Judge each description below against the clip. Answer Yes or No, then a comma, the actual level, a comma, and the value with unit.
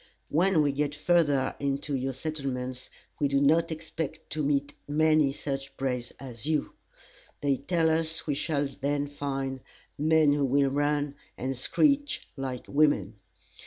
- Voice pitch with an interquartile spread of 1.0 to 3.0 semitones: Yes, narrow, 2.4 semitones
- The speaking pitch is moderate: Yes, medium, 145 Hz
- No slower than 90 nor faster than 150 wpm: Yes, average, 145 wpm